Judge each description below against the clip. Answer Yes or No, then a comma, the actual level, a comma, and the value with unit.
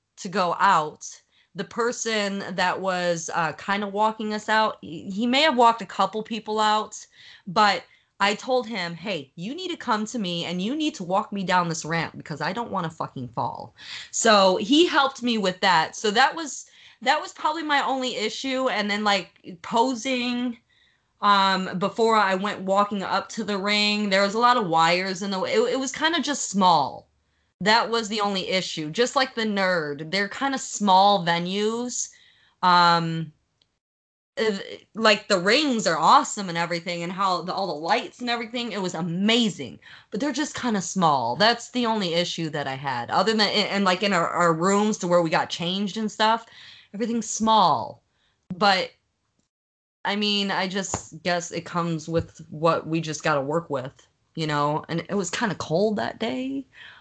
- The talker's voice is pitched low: No, high, 205 Hz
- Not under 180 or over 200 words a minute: Yes, average, 190 wpm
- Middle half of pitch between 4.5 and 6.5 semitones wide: Yes, average, 4.9 semitones